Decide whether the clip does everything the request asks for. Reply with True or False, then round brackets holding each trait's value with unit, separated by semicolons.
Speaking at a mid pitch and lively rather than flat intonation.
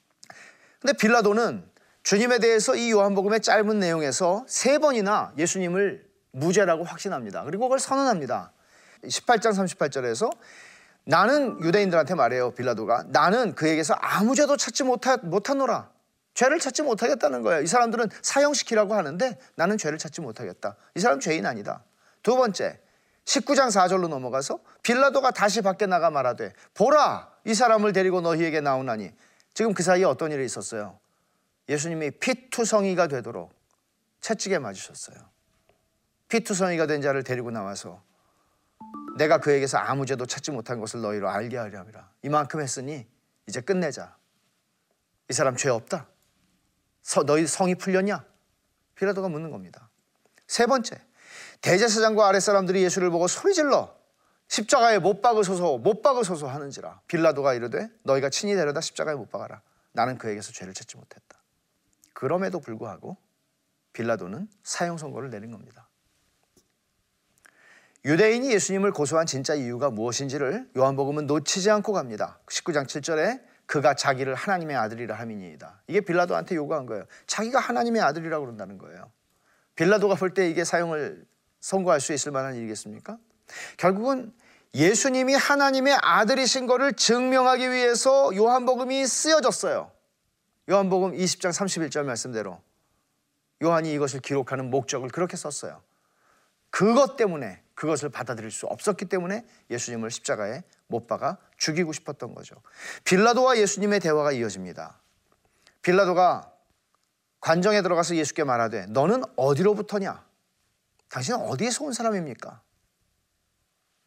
True (180 Hz; 8.1 semitones)